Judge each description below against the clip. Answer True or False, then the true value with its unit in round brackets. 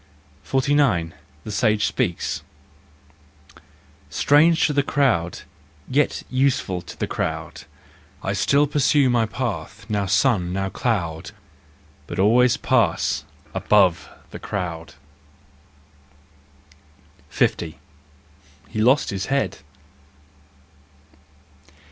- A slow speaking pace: True (90 wpm)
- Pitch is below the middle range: True (110 Hz)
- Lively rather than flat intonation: True (6.9 semitones)